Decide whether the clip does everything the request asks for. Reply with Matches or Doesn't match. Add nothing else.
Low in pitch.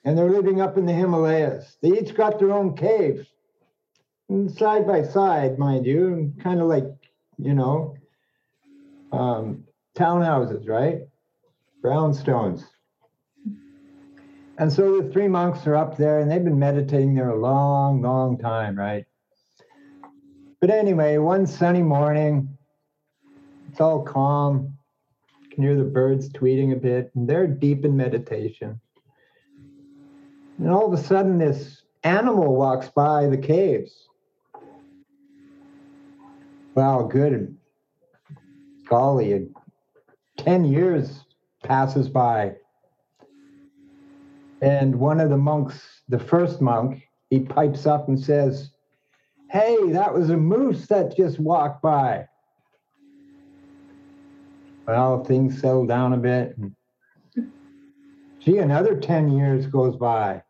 Doesn't match